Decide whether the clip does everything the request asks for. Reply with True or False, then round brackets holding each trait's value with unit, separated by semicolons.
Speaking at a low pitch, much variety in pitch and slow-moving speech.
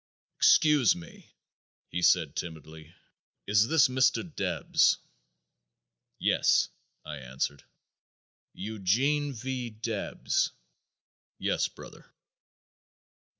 True (110 Hz; 7.5 semitones; 75 wpm)